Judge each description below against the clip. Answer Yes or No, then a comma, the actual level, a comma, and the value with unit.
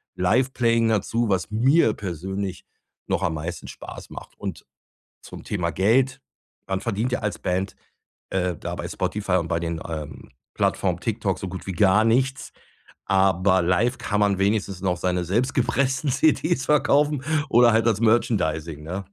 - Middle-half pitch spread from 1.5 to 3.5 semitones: No, average, 4.7 semitones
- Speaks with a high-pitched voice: No, low, 100 Hz